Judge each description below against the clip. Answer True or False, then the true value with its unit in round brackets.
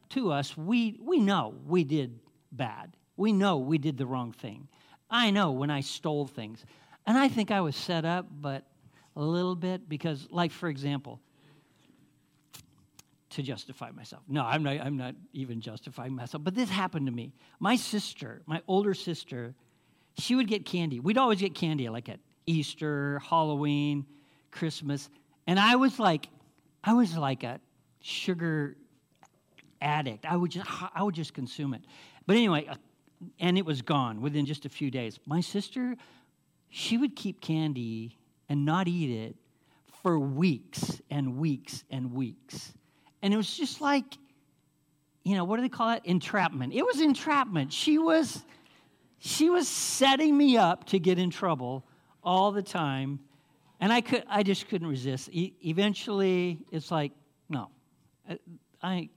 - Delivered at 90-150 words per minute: False (160 wpm)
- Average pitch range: False (5.7 semitones)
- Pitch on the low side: False (160 Hz)